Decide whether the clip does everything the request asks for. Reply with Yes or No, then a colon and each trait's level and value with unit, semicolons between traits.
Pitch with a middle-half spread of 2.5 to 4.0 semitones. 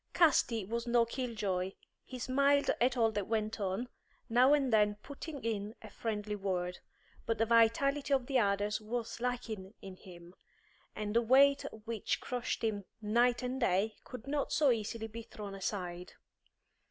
Yes: average, 3.3 semitones